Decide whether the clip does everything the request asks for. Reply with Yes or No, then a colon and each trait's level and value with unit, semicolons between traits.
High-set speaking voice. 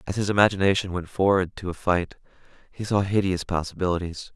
No: very low, 95 Hz